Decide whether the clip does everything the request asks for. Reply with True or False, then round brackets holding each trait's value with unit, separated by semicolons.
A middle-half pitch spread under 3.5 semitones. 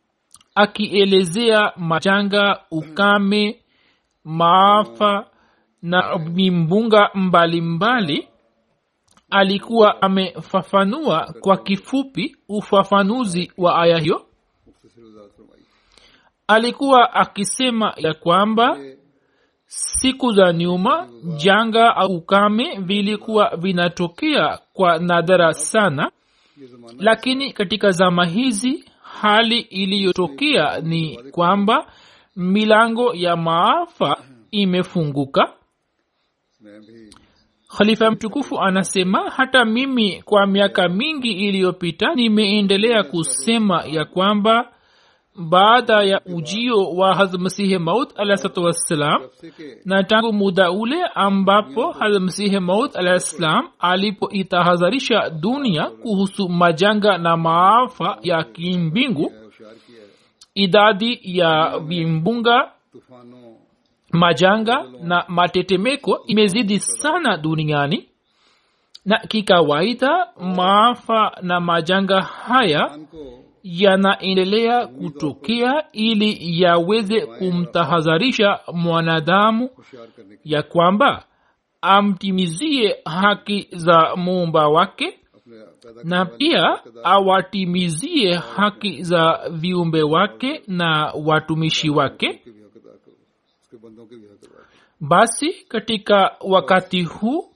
False (4.1 semitones)